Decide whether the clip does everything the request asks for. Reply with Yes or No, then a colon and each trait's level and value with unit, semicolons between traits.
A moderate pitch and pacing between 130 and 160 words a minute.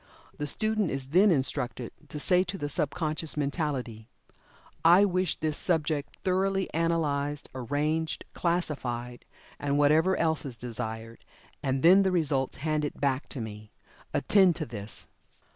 Yes: medium, 150 Hz; average, 140 wpm